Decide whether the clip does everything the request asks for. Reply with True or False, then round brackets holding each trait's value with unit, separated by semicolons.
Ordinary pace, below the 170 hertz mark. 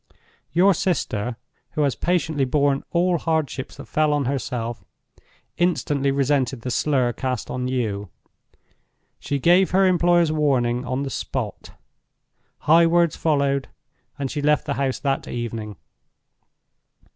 False (120 wpm; 140 Hz)